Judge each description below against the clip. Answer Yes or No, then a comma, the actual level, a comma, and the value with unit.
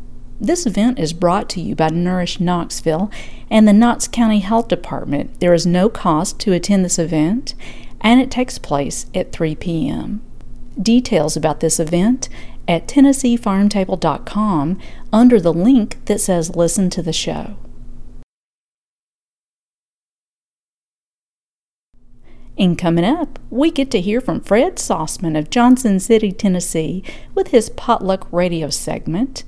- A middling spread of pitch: No, wide, 5.7 semitones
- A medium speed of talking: No, slow, 130 wpm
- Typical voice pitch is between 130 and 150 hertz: No, high, 190 Hz